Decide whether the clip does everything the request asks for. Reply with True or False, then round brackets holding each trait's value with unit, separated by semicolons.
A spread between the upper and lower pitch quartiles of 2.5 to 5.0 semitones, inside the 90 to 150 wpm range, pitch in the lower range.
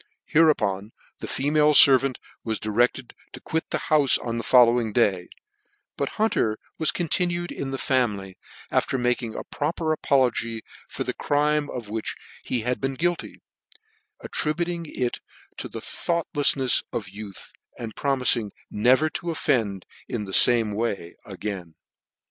False (5.5 semitones; 145 wpm; 125 Hz)